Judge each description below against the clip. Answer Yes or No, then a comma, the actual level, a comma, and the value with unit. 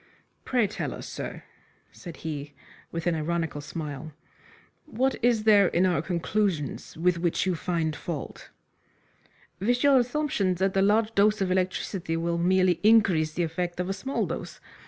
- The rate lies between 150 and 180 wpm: Yes, average, 155 wpm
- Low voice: No, medium, 180 Hz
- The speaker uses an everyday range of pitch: Yes, average, 4.2 semitones